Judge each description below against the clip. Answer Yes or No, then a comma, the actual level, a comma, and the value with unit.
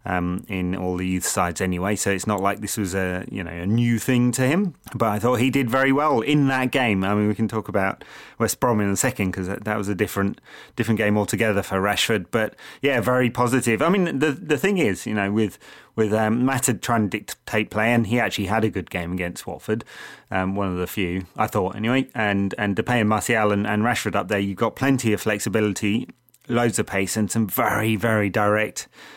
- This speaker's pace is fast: Yes, fast, 235 wpm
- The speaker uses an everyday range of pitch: Yes, average, 3.3 semitones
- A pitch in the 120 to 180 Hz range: No, low, 105 Hz